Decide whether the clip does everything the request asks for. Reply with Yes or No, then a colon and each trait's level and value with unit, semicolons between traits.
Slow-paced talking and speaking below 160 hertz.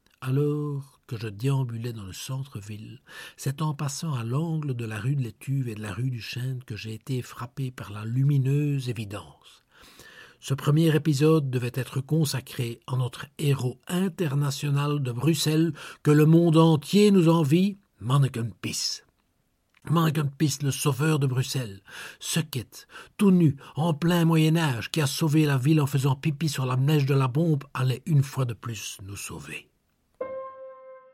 No: average, 160 wpm; medium, 140 Hz